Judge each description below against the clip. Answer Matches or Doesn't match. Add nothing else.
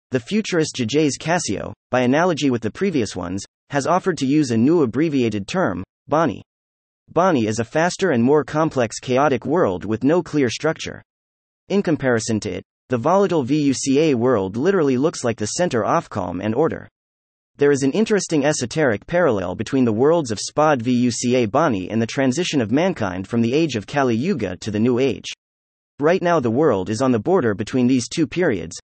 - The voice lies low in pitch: Matches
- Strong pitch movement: Matches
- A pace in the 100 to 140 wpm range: Doesn't match